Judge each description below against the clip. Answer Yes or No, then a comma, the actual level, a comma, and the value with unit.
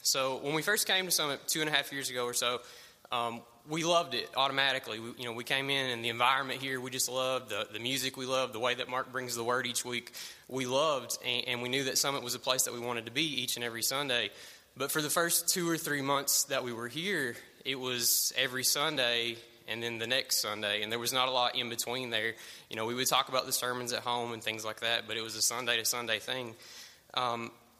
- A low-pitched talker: Yes, low, 125 Hz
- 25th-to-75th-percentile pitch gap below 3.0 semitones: Yes, narrow, 2.4 semitones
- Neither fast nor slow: No, fast, 260 wpm